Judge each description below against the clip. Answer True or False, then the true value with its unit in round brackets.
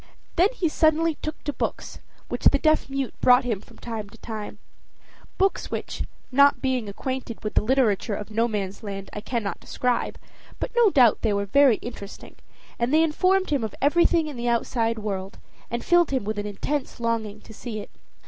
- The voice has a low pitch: False (235 Hz)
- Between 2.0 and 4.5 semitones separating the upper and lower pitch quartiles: False (5.2 semitones)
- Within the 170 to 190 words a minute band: True (185 wpm)